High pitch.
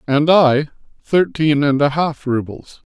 No: medium, 145 Hz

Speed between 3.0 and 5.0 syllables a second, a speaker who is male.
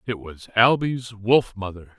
Yes: 4.0 syllables/s; male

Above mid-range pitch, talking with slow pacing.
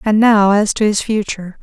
No: high, 210 Hz; fast, 220 wpm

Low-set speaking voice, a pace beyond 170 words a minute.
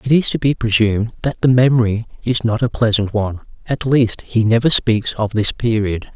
Yes: low, 115 Hz; fast, 205 wpm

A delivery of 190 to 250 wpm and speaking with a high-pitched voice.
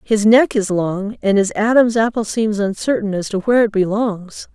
Yes: average, 200 wpm; high, 210 Hz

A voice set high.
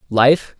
No: low, 135 Hz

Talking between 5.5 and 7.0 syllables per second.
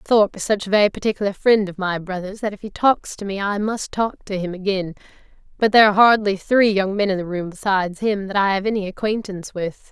Yes: 6.1 syllables/s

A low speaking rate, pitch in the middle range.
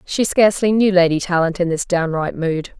No: average, 195 wpm; medium, 180 Hz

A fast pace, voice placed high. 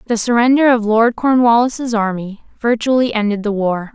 No: average, 150 wpm; high, 225 Hz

